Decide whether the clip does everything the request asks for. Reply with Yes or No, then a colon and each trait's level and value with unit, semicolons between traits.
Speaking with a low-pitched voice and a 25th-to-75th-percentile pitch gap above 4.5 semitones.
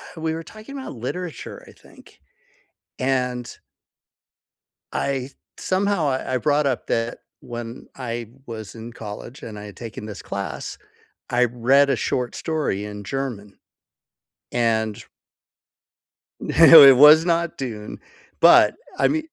Yes: low, 125 Hz; average, 5.1 semitones